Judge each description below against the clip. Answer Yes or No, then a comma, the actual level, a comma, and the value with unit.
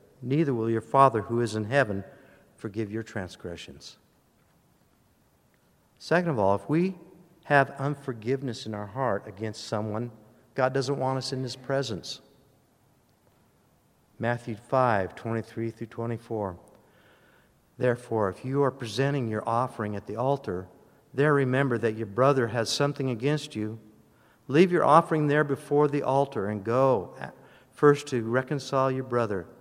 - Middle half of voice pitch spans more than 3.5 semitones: Yes, average, 3.9 semitones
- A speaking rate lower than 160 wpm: Yes, average, 140 wpm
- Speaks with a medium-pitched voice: No, low, 125 Hz